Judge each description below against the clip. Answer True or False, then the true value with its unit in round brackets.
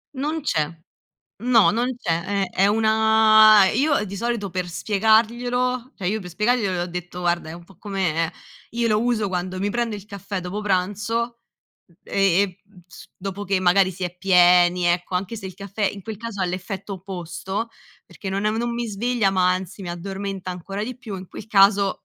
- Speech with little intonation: False (3.3 semitones)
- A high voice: True (200 Hz)